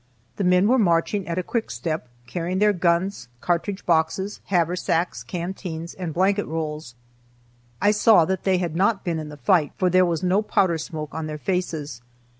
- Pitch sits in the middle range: Yes, medium, 175 Hz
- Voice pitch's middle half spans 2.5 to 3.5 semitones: Yes, average, 3.0 semitones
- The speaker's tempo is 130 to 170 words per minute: No, average, 180 wpm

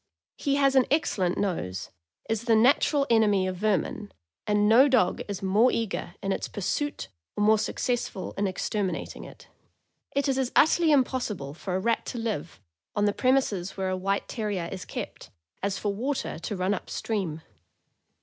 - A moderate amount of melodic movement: Yes, average, 4.9 semitones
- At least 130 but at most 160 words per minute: No, average, 180 wpm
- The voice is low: No, high, 210 Hz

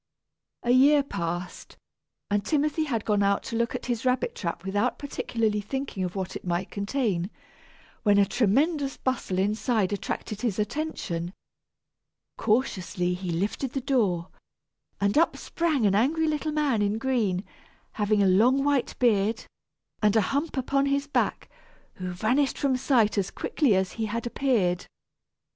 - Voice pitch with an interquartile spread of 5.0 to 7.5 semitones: Yes, wide, 5.5 semitones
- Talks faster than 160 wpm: No, average, 155 wpm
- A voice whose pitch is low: No, high, 220 Hz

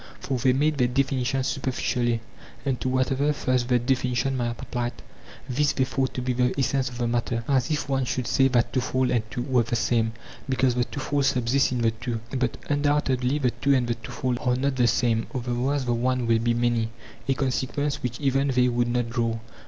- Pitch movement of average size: No, narrow, 1.9 semitones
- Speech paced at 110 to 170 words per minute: No, fast, 205 wpm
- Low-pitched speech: Yes, low, 125 Hz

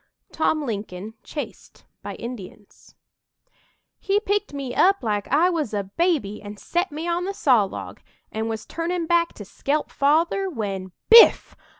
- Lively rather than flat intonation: Yes, wide, 8.5 semitones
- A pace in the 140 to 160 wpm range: Yes, average, 150 wpm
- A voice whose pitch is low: No, very high, 285 Hz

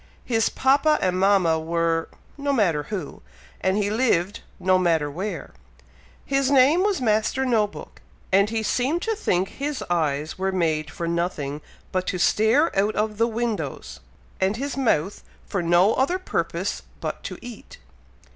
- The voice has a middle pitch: No, high, 205 Hz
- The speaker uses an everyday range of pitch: No, wide, 6.8 semitones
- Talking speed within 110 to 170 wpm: Yes, average, 155 wpm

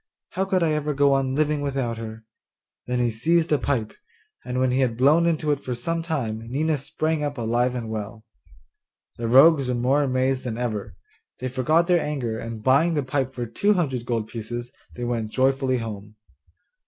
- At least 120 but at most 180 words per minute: No, average, 190 wpm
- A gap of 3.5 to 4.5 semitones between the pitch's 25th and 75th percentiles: Yes, average, 3.9 semitones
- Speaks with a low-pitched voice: Yes, low, 130 Hz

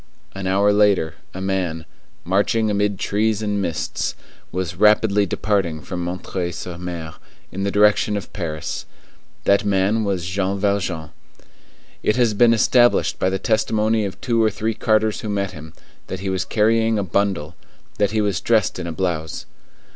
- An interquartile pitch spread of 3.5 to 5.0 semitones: No, average, 2.8 semitones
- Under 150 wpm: No, average, 165 wpm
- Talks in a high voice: No, low, 100 Hz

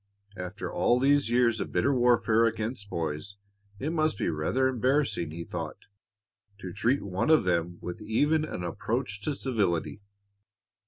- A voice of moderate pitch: No, low, 110 Hz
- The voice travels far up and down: Yes, wide, 6.3 semitones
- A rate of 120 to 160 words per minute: Yes, average, 150 wpm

